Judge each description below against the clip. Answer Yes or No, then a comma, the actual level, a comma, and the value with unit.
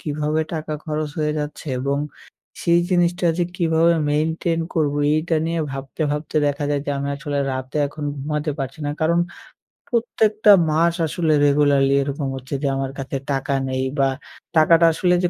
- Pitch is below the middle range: No, medium, 150 Hz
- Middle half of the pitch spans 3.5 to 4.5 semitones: No, average, 2.9 semitones